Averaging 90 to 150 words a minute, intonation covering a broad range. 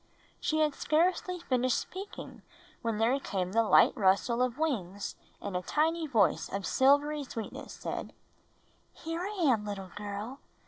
Yes: average, 145 wpm; wide, 7.1 semitones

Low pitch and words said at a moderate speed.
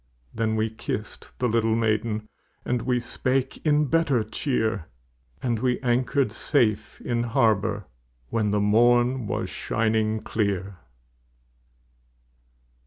No: low, 115 Hz; slow, 110 wpm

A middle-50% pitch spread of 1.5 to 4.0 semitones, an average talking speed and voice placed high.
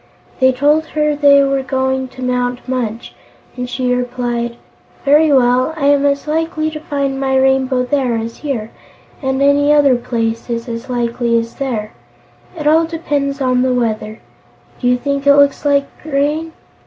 Yes: narrow, 2.5 semitones; average, 165 wpm; very high, 265 Hz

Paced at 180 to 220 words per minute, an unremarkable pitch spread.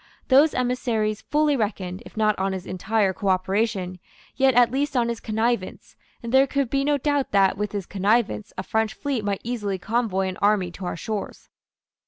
Yes: average, 185 wpm; average, 4.3 semitones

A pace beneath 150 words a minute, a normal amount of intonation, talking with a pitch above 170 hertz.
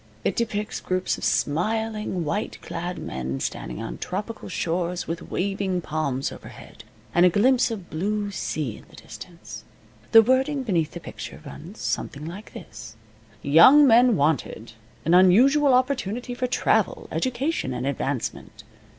No: average, 140 wpm; wide, 6.5 semitones; medium, 185 Hz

